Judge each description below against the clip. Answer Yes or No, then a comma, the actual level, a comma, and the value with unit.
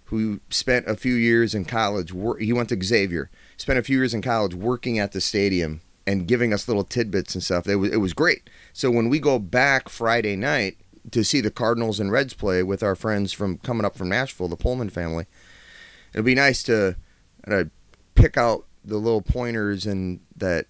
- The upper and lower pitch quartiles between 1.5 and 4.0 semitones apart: Yes, average, 3.7 semitones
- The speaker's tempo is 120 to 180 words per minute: No, average, 200 wpm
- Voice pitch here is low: Yes, low, 105 Hz